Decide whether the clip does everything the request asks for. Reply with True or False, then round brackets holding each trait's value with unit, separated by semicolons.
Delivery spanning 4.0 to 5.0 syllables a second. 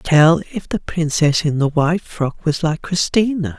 True (4.3 syllables/s)